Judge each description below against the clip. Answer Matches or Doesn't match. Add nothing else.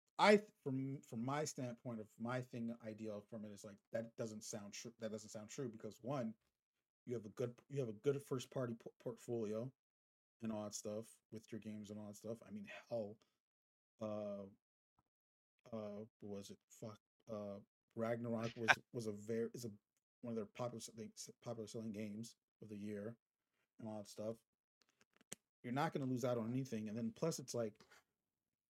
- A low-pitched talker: Matches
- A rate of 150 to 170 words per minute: Doesn't match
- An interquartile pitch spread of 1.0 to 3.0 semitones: Matches